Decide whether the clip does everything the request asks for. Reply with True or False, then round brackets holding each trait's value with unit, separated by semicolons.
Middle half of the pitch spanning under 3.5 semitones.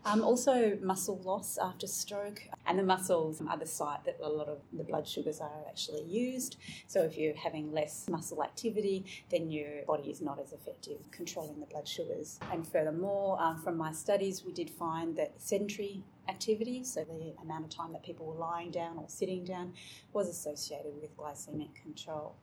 False (4.2 semitones)